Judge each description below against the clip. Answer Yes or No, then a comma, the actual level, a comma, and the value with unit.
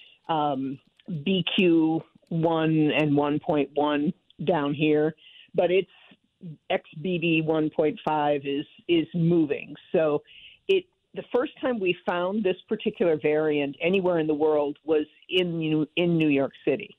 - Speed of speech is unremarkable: No, slow, 125 wpm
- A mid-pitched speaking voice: Yes, medium, 160 Hz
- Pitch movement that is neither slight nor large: Yes, average, 3.2 semitones